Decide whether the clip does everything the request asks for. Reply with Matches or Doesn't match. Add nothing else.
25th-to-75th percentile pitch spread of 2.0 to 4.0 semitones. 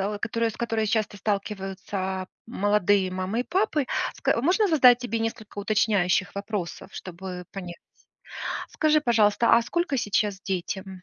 Matches